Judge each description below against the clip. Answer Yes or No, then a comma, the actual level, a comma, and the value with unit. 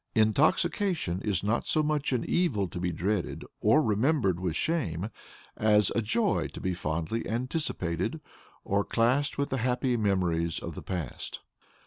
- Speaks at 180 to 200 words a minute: No, average, 150 wpm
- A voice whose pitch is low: Yes, low, 110 Hz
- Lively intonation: Yes, wide, 7.0 semitones